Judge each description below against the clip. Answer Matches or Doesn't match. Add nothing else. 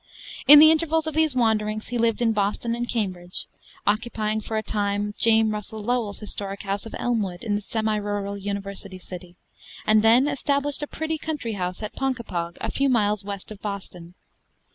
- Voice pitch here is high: Matches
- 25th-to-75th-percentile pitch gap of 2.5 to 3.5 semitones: Matches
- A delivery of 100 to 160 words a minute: Doesn't match